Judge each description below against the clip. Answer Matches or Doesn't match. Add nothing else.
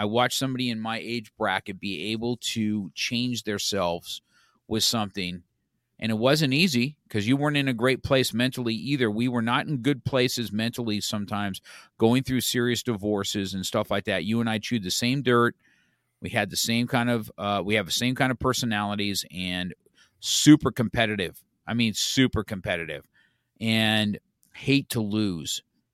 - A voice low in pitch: Matches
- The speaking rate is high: Doesn't match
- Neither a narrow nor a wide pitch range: Matches